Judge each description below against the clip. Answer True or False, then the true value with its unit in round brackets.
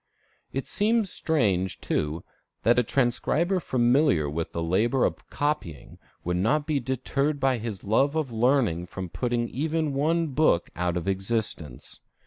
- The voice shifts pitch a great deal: True (7.8 semitones)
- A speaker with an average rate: True (145 wpm)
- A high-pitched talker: False (120 Hz)